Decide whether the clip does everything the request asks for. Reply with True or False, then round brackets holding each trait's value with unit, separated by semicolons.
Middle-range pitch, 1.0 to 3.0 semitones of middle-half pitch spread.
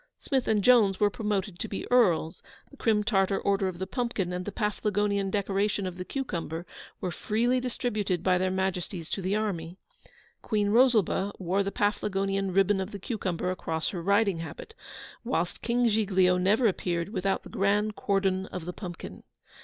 False (195 Hz; 2.4 semitones)